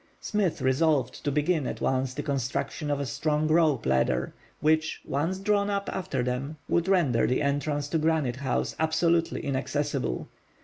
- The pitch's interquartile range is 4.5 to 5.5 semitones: No, average, 3.3 semitones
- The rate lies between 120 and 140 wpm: No, average, 160 wpm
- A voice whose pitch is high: No, medium, 150 Hz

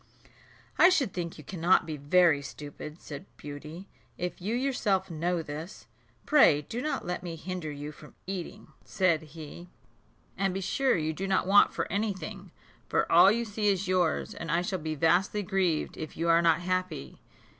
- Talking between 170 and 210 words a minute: Yes, average, 180 wpm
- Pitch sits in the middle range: Yes, medium, 175 Hz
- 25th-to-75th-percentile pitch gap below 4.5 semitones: Yes, average, 3.6 semitones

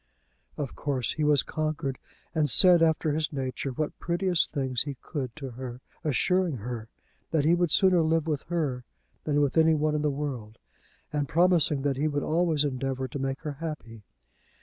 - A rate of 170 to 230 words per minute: Yes, average, 180 wpm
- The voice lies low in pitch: No, medium, 150 Hz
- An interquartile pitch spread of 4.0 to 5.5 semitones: No, average, 3.2 semitones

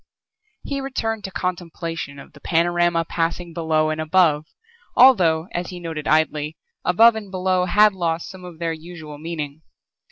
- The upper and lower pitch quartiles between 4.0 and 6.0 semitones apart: No, narrow, 2.6 semitones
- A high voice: No, medium, 170 Hz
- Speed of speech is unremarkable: Yes, average, 155 wpm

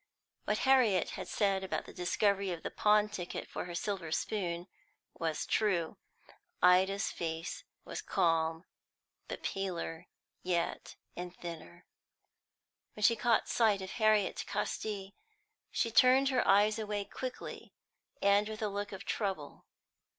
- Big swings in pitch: No, average, 3.4 semitones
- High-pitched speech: Yes, high, 195 Hz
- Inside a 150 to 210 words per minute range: No, slow, 135 wpm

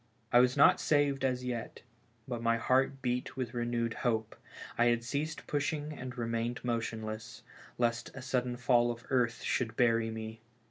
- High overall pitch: No, low, 120 Hz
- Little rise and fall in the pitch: Yes, narrow, 1.8 semitones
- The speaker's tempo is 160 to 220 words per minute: Yes, average, 170 wpm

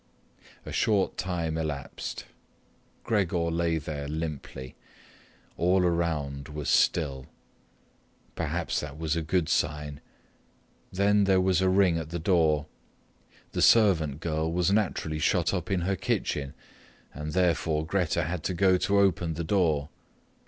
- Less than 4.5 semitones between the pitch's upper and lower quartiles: Yes, average, 3.3 semitones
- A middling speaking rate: No, slow, 130 wpm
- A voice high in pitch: No, very low, 85 Hz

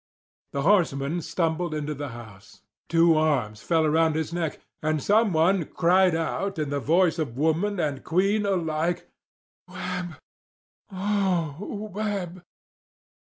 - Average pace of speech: No, slow, 120 wpm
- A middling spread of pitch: Yes, average, 3.4 semitones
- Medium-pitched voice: Yes, medium, 165 Hz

